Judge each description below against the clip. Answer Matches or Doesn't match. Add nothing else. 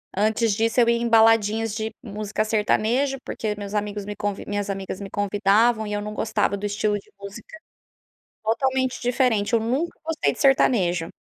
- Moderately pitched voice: Doesn't match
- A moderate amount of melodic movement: Doesn't match